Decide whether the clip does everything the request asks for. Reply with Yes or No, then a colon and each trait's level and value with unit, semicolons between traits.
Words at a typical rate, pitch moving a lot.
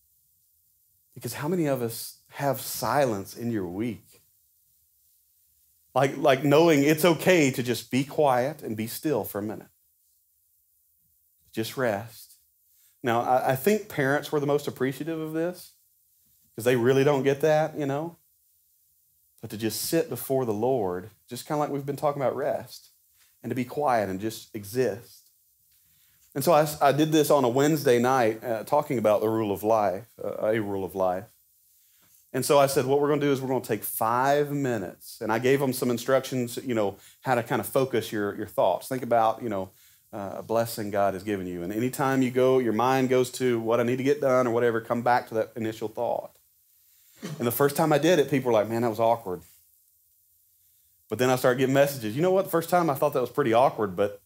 No: fast, 210 wpm; wide, 6.6 semitones